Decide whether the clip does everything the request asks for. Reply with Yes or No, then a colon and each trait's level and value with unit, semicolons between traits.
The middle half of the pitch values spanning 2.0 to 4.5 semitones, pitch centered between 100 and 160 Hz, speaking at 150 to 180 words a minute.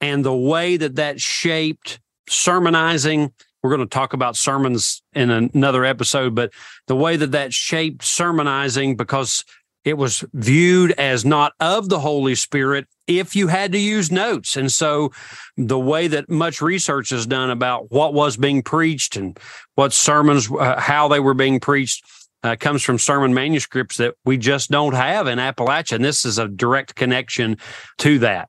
Yes: average, 3.2 semitones; medium, 140 Hz; average, 175 wpm